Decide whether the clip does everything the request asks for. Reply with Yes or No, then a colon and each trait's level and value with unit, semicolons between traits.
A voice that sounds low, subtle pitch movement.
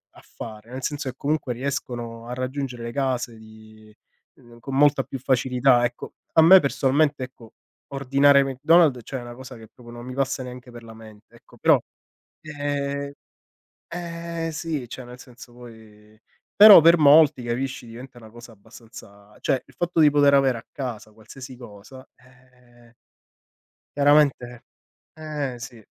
No: low, 125 Hz; average, 3.1 semitones